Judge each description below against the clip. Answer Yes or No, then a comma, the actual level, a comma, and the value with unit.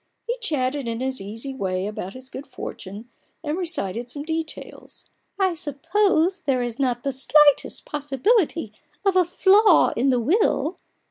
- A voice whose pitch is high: Yes, very high, 280 Hz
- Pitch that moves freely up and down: Yes, wide, 5.9 semitones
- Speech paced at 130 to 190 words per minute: Yes, average, 155 wpm